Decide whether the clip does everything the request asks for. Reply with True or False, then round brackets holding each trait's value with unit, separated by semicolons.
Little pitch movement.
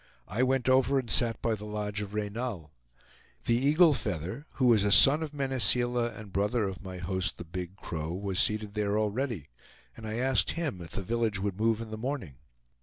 False (4.3 semitones)